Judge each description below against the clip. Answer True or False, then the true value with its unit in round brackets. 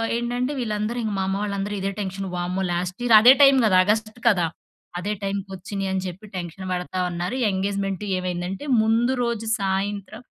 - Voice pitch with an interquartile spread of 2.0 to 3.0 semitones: True (2.7 semitones)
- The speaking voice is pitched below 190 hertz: False (195 Hz)